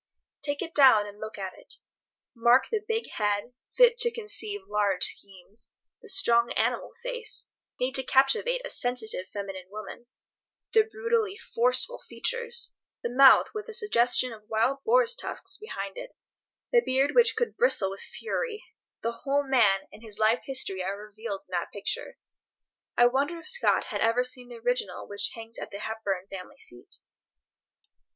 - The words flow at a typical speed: Yes, average, 160 wpm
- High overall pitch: Yes, very high, 250 Hz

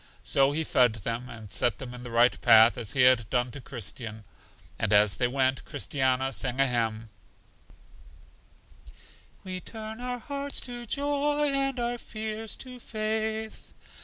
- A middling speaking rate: Yes, average, 155 wpm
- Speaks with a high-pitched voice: No, low, 135 Hz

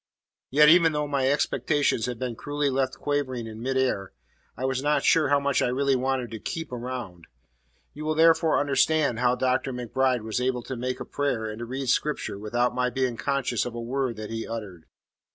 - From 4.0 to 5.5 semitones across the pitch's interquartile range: No, average, 3.0 semitones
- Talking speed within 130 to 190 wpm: No, fast, 205 wpm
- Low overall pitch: Yes, low, 130 Hz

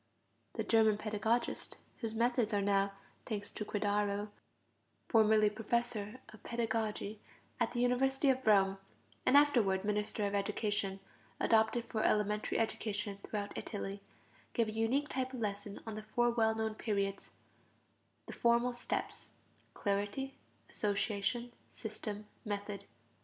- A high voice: Yes, high, 215 Hz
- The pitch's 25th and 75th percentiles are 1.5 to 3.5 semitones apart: Yes, narrow, 2.5 semitones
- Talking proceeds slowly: Yes, slow, 125 wpm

